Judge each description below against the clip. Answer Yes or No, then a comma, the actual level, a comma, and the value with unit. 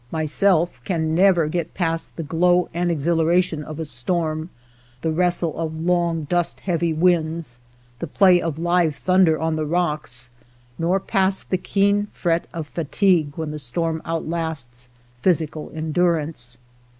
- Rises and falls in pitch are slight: Yes, narrow, 2.2 semitones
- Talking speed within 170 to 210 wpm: No, average, 140 wpm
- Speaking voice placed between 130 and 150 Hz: No, medium, 165 Hz